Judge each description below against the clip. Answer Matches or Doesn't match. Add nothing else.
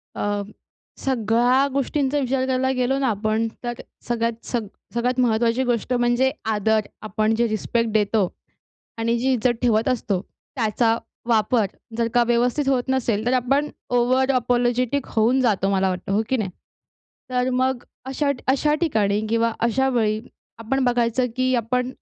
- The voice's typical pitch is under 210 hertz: Doesn't match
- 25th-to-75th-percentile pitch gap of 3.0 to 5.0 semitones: Doesn't match